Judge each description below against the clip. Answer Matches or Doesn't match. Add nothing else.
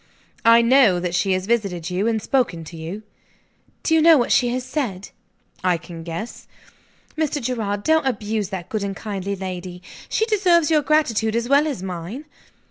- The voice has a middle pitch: Doesn't match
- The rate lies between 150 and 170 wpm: Doesn't match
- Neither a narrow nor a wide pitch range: Doesn't match